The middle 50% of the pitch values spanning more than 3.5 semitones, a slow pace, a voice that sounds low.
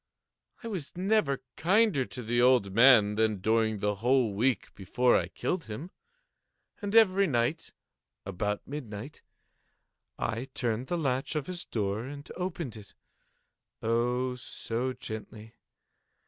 Yes: wide, 5.5 semitones; slow, 125 wpm; low, 125 Hz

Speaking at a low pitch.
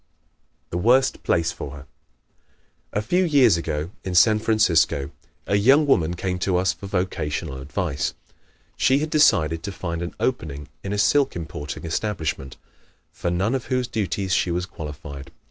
Yes: very low, 90 Hz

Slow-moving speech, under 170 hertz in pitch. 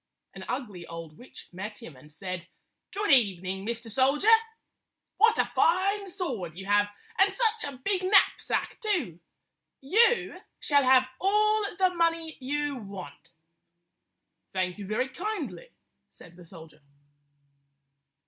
No: slow, 130 wpm; very high, 260 Hz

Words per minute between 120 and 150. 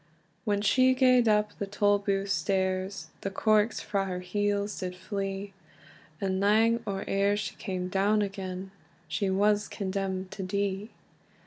Yes: average, 140 wpm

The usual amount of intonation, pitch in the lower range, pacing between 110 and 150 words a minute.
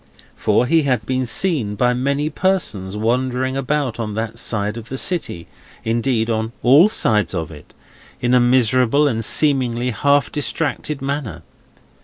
Yes: average, 4.0 semitones; low, 125 Hz; average, 140 wpm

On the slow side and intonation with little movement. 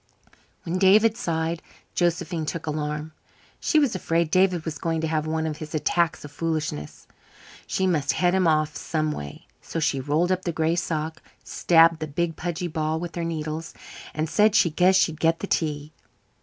No: average, 180 wpm; narrow, 2.1 semitones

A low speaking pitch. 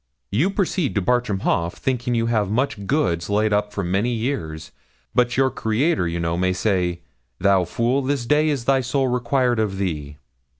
Yes: low, 110 Hz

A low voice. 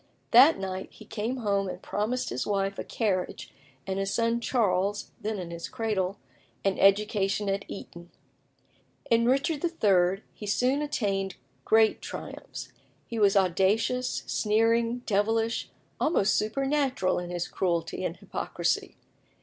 No: high, 210 Hz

